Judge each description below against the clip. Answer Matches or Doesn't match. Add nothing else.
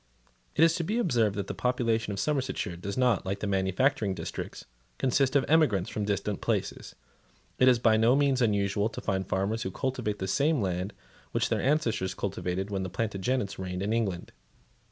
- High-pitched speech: Doesn't match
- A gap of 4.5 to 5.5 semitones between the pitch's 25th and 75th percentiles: Matches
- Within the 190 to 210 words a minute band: Matches